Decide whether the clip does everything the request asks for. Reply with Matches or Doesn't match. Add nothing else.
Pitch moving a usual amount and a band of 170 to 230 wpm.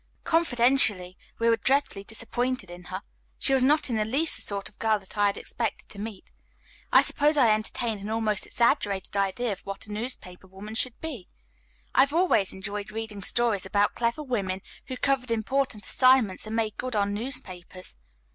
Matches